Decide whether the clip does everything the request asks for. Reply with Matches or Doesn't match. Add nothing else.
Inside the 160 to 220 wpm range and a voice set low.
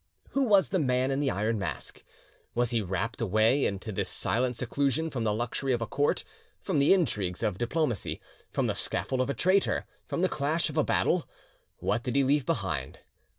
Matches